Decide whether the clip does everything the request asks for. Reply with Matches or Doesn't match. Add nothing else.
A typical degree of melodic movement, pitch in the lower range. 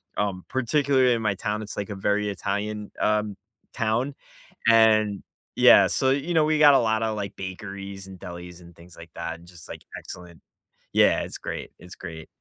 Matches